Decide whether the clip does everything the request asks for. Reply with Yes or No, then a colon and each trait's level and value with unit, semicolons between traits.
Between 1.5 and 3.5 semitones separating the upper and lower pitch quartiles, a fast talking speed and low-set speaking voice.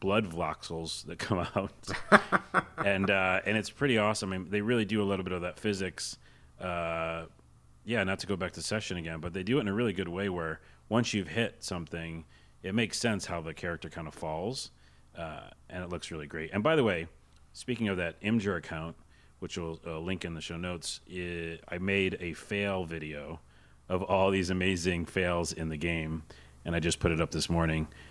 Yes: average, 3.2 semitones; fast, 210 wpm; very low, 85 Hz